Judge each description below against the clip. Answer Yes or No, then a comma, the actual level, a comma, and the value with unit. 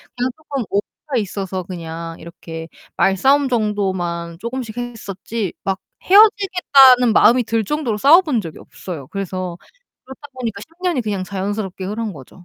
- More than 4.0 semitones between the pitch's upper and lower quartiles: Yes, wide, 5.4 semitones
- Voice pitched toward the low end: No, high, 210 Hz